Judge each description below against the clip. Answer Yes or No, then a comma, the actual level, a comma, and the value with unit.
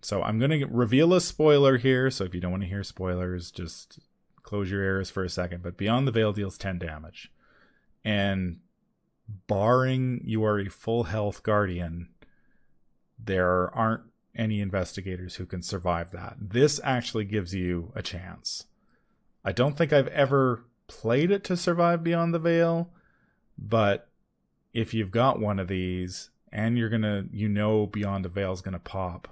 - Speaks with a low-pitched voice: Yes, low, 105 Hz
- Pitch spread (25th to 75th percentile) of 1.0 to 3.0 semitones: No, average, 4.9 semitones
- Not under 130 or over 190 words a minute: Yes, average, 170 wpm